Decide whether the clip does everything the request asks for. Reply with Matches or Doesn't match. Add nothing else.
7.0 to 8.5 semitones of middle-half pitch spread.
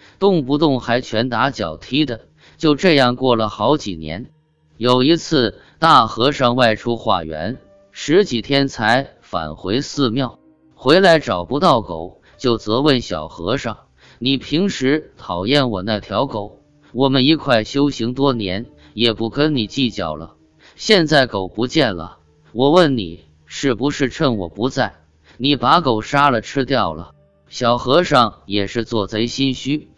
Doesn't match